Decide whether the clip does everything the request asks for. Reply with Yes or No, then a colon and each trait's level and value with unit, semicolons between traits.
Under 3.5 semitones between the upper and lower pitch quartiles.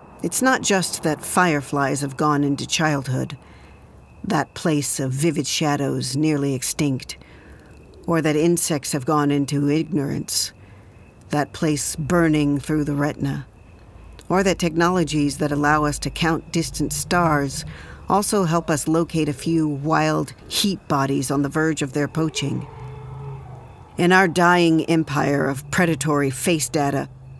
Yes: average, 2.8 semitones